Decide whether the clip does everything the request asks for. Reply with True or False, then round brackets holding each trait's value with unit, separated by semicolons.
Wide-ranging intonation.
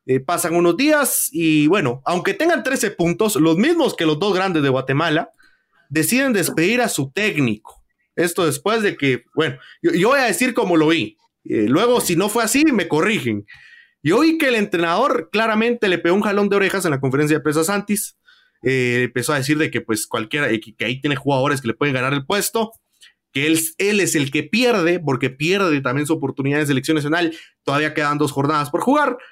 True (7.1 semitones)